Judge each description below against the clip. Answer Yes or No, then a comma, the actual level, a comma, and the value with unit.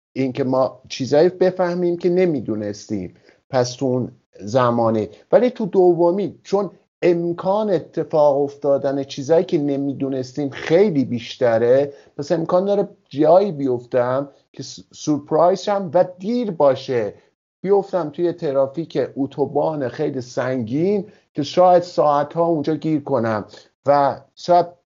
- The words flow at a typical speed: Yes, average, 115 wpm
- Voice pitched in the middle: Yes, medium, 150 Hz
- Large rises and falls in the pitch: No, average, 5.0 semitones